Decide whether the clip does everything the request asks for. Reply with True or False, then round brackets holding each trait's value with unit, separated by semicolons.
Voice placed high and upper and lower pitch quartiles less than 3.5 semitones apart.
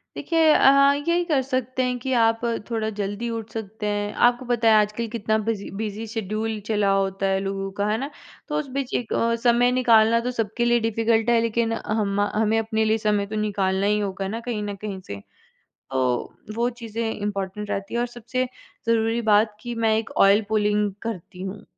True (220 Hz; 2.4 semitones)